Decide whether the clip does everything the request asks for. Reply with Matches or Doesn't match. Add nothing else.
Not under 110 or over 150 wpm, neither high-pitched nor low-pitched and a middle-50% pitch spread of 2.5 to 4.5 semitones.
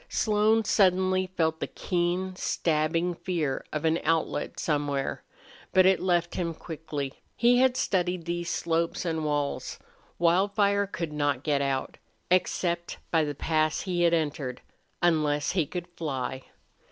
Matches